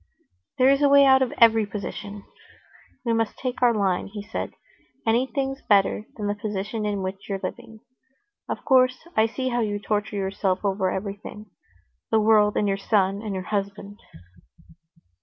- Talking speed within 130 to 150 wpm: No, average, 160 wpm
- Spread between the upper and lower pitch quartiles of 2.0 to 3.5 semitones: Yes, narrow, 2.6 semitones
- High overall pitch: Yes, high, 210 Hz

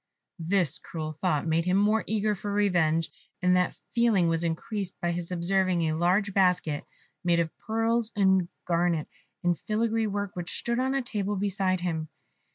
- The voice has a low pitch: No, medium, 185 Hz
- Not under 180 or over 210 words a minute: No, average, 165 wpm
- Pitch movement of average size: Yes, average, 3.4 semitones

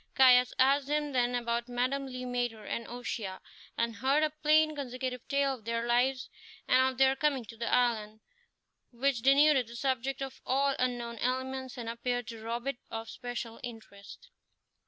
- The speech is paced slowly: No, average, 170 wpm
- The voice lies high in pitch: Yes, very high, 250 Hz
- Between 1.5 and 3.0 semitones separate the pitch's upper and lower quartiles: Yes, narrow, 2.4 semitones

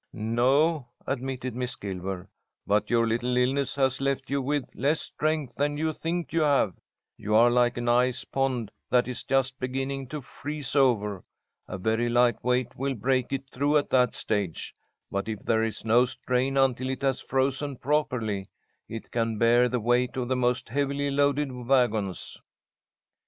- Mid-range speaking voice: No, low, 125 Hz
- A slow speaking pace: No, average, 170 wpm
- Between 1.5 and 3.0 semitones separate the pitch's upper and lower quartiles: Yes, narrow, 2.6 semitones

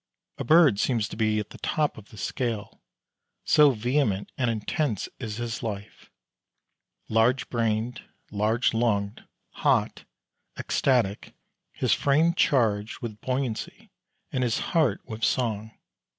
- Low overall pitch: Yes, low, 115 Hz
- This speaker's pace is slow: Yes, slow, 125 wpm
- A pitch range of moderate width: Yes, average, 3.6 semitones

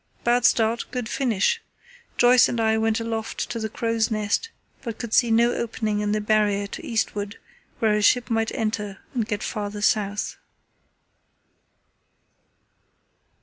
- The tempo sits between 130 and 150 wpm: Yes, average, 145 wpm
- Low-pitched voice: No, high, 220 Hz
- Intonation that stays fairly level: Yes, narrow, 1.8 semitones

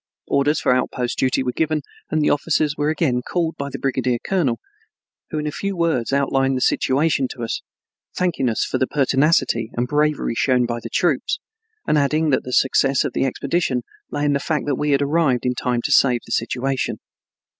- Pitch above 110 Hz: Yes, medium, 140 Hz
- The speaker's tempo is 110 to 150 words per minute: No, average, 200 wpm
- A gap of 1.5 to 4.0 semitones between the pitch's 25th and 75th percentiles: Yes, average, 3.2 semitones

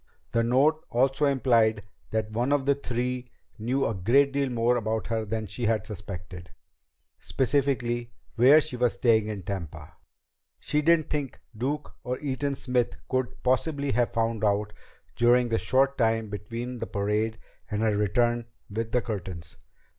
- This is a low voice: Yes, low, 120 Hz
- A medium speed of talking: Yes, average, 155 wpm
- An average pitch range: Yes, average, 3.3 semitones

